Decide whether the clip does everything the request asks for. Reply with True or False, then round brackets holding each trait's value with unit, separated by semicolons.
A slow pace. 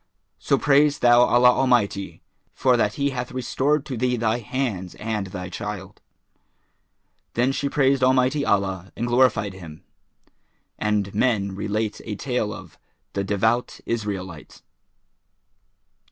True (130 wpm)